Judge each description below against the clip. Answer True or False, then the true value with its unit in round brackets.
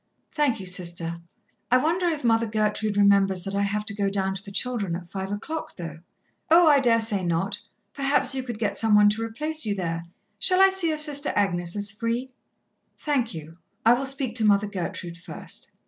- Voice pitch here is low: False (210 Hz)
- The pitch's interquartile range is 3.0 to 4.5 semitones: False (5.3 semitones)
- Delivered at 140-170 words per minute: False (205 wpm)